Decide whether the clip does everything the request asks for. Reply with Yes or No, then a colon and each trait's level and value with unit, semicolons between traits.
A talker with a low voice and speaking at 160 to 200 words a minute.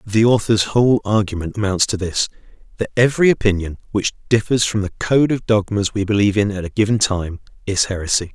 Yes: low, 105 Hz; average, 185 wpm